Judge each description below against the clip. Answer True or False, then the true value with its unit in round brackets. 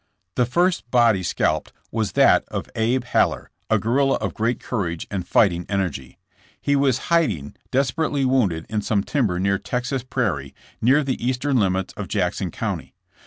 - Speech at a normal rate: True (165 wpm)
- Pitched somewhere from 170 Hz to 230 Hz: False (115 Hz)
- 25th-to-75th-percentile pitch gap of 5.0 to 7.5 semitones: True (5.6 semitones)